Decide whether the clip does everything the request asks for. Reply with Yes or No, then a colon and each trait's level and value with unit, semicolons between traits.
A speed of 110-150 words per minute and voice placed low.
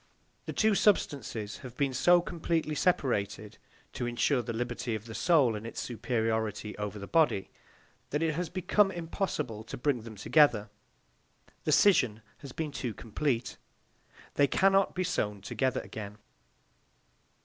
Yes: average, 145 wpm; low, 125 Hz